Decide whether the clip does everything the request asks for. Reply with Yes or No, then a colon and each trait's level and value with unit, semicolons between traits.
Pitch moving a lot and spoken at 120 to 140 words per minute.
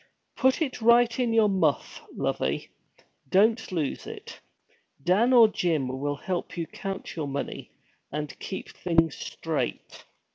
Yes: wide, 6.7 semitones; slow, 135 wpm